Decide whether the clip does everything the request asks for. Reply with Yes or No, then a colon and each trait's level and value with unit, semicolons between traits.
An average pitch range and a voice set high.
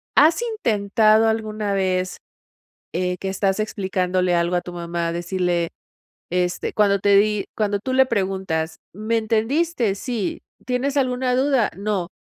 Yes: average, 3.9 semitones; high, 200 Hz